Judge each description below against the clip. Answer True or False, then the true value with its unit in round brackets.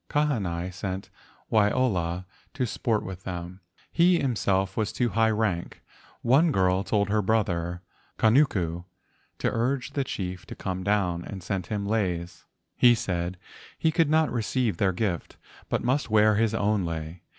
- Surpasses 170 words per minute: False (155 wpm)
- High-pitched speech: False (100 Hz)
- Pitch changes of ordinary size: True (4.2 semitones)